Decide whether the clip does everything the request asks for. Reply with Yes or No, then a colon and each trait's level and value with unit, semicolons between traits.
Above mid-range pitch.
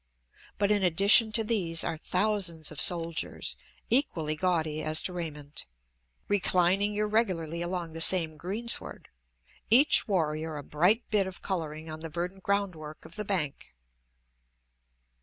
No: medium, 175 Hz